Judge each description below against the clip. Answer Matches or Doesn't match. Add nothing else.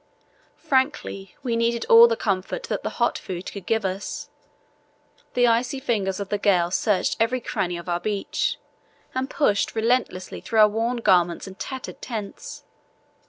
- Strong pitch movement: Doesn't match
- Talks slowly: Doesn't match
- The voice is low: Doesn't match